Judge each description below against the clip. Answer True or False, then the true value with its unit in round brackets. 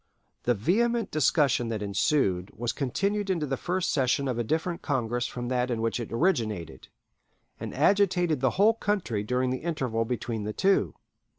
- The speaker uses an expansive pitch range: True (7.4 semitones)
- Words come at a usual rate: True (170 wpm)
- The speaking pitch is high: False (130 Hz)